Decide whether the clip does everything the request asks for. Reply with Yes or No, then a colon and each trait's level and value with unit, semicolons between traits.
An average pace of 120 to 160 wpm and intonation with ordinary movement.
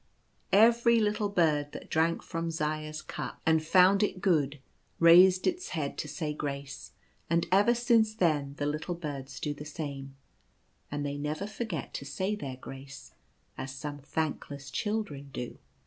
Yes: average, 155 wpm; average, 4.9 semitones